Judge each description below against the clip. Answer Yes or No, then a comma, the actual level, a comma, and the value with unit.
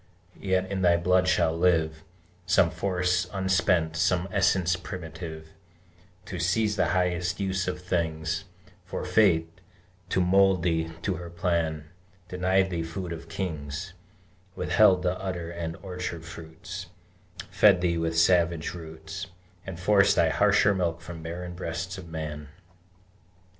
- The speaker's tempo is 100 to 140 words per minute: Yes, slow, 135 wpm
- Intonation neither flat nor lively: No, narrow, 2.2 semitones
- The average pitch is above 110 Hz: No, very low, 90 Hz